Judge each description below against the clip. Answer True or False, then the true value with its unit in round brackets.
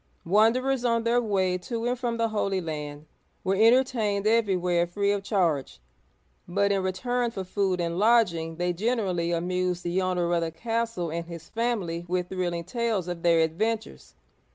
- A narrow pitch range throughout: False (4.8 semitones)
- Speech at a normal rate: True (165 wpm)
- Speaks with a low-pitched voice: False (190 Hz)